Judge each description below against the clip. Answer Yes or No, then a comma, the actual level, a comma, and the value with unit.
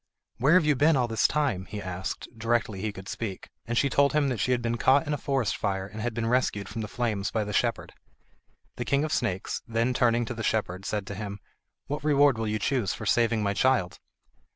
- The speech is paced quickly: Yes, fast, 240 wpm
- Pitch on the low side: Yes, low, 115 Hz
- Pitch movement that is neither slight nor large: Yes, average, 4.2 semitones